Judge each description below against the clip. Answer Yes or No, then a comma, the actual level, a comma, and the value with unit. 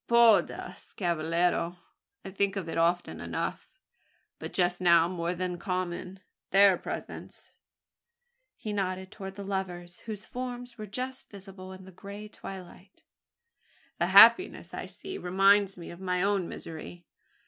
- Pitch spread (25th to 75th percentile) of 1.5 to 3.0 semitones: Yes, narrow, 2.6 semitones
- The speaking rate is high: No, average, 145 wpm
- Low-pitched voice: No, high, 190 Hz